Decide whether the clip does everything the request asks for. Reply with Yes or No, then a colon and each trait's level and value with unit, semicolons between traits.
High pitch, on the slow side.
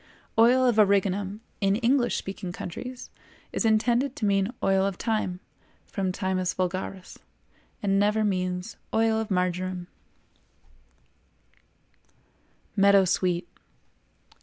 Yes: high, 195 Hz; slow, 105 wpm